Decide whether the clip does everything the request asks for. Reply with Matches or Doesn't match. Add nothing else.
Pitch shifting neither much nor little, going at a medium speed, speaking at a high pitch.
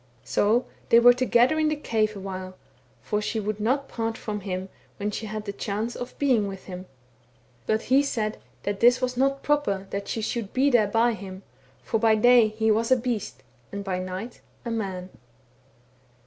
Matches